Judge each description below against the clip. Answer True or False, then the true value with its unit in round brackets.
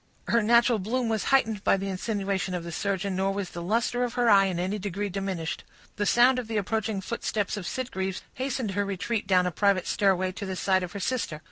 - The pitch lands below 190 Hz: False (200 Hz)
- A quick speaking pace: True (225 wpm)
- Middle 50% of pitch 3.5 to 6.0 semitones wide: False (3.1 semitones)